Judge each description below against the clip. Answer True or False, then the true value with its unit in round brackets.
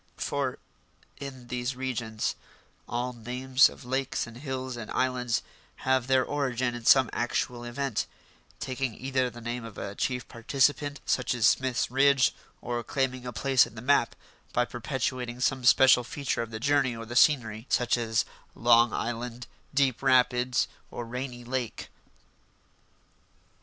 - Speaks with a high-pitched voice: False (125 Hz)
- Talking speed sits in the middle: True (145 wpm)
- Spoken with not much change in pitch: True (1.8 semitones)